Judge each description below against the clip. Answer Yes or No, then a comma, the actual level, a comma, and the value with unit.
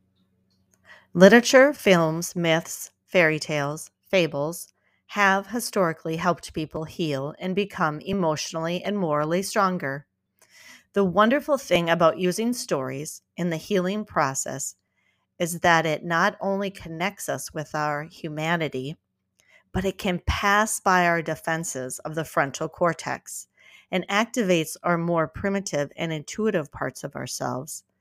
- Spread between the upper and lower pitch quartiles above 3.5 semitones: Yes, average, 4.2 semitones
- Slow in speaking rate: Yes, slow, 125 wpm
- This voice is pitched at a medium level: Yes, medium, 170 Hz